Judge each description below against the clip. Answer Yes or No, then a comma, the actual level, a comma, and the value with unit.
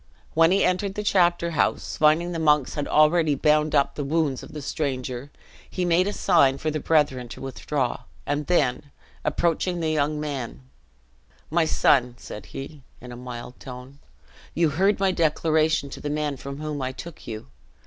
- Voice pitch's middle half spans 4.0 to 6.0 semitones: No, average, 3.5 semitones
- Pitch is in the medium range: Yes, medium, 150 Hz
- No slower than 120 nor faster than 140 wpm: No, average, 180 wpm